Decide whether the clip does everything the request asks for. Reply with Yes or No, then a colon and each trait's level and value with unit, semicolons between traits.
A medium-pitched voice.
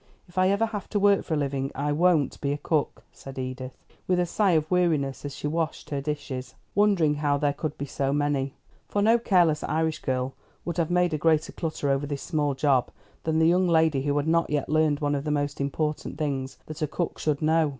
Yes: medium, 150 Hz